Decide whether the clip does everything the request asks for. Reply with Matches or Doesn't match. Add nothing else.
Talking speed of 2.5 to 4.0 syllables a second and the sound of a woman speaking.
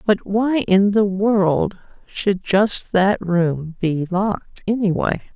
Matches